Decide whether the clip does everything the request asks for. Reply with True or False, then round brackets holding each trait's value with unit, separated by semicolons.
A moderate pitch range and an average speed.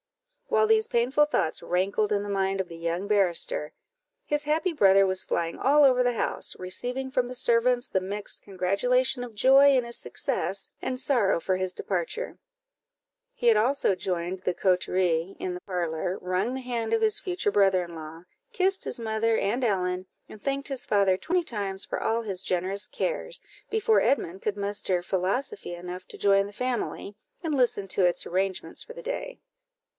False (6.1 semitones; 180 wpm)